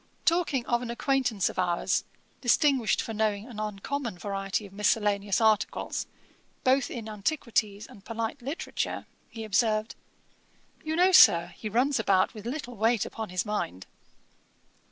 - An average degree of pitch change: Yes, average, 3.5 semitones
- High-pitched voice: Yes, high, 220 Hz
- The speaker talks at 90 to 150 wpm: Yes, average, 140 wpm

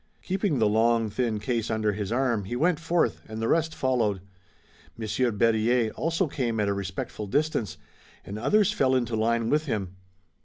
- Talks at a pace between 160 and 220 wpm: Yes, average, 170 wpm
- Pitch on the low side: Yes, low, 115 Hz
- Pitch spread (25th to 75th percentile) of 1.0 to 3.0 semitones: No, average, 3.9 semitones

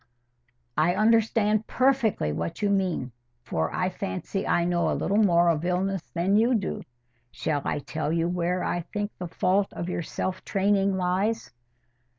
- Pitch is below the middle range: No, medium, 185 Hz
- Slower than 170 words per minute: Yes, average, 160 wpm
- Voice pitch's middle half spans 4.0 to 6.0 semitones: No, average, 3.2 semitones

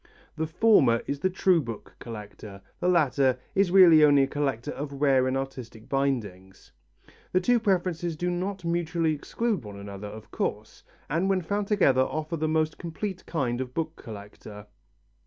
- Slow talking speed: No, average, 165 wpm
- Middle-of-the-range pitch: Yes, medium, 150 Hz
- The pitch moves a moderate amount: No, wide, 6.1 semitones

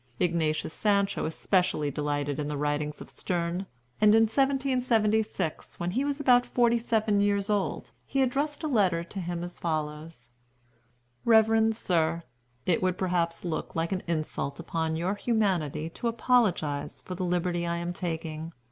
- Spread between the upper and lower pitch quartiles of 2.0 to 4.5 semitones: No, average, 5.3 semitones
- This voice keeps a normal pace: Yes, average, 155 wpm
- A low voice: No, medium, 180 Hz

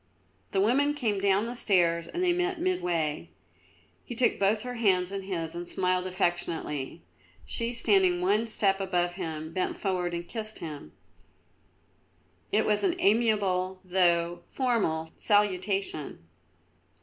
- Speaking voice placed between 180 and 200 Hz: Yes, high, 190 Hz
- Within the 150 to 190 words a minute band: No, slow, 135 wpm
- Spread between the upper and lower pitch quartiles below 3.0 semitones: No, average, 4.0 semitones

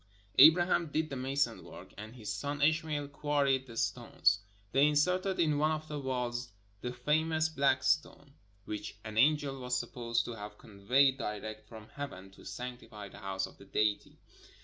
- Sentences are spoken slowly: No, average, 170 wpm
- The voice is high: No, low, 130 Hz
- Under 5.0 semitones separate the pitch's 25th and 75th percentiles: No, average, 5.3 semitones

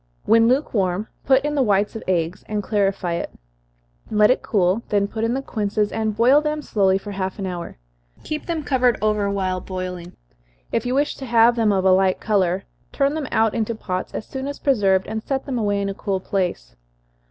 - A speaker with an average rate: No, fast, 210 wpm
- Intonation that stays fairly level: No, average, 4.2 semitones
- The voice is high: Yes, high, 210 Hz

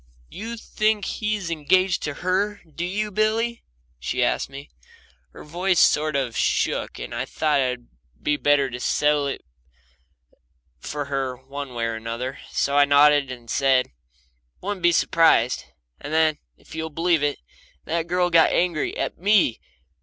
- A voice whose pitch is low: No, medium, 150 Hz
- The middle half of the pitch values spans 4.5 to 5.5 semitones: Yes, average, 4.9 semitones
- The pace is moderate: Yes, average, 155 wpm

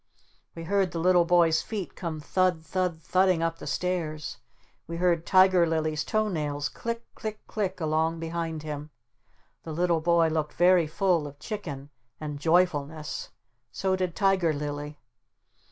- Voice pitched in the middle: Yes, medium, 165 Hz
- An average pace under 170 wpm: Yes, average, 150 wpm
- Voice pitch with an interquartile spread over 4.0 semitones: No, average, 2.9 semitones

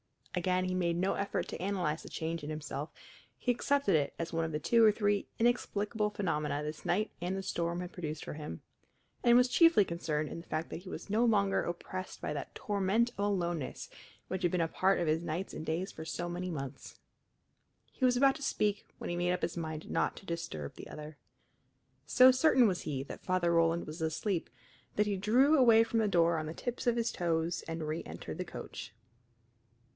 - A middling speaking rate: No, fast, 210 wpm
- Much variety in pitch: No, average, 4.5 semitones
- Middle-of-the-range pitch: Yes, medium, 180 Hz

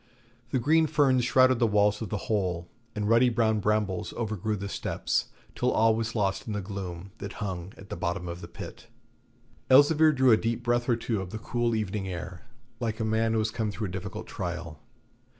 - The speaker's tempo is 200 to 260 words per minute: Yes, fast, 205 wpm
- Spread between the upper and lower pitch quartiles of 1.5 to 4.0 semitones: Yes, average, 3.6 semitones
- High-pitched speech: No, low, 110 Hz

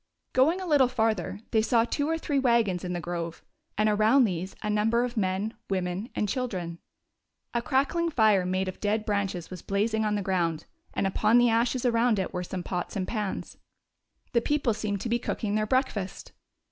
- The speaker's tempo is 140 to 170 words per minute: No, average, 195 wpm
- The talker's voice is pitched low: No, high, 215 Hz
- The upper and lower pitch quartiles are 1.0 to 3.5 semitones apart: No, average, 4.2 semitones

